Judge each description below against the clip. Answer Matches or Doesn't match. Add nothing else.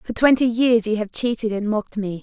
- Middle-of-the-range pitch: Doesn't match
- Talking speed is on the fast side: Matches